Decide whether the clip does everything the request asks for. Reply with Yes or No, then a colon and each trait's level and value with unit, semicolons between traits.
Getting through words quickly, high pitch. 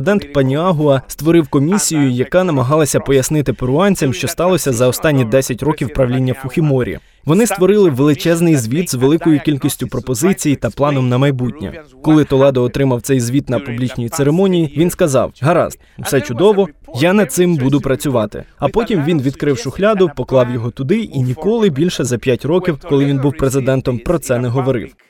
No: fast, 165 wpm; medium, 140 Hz